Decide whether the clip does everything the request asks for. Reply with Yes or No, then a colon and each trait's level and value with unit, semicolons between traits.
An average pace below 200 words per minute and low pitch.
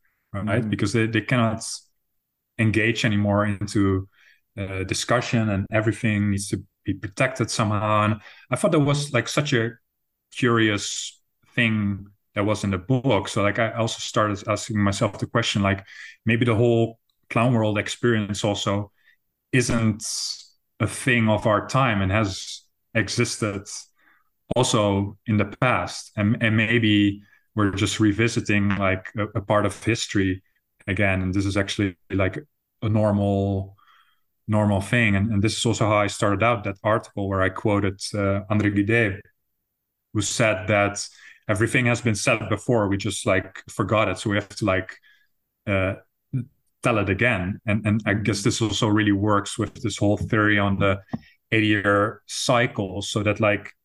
Yes: average, 160 wpm; low, 105 Hz